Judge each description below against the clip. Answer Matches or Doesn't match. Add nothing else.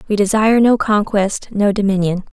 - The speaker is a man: Doesn't match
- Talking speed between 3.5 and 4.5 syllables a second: Doesn't match